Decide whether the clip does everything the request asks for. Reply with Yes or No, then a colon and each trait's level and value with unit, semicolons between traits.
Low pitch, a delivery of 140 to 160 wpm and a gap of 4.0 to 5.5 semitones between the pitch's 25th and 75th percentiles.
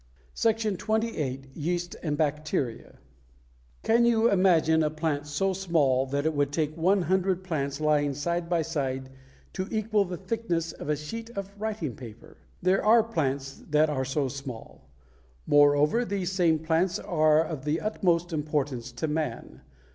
No: medium, 160 Hz; average, 155 wpm; average, 4.6 semitones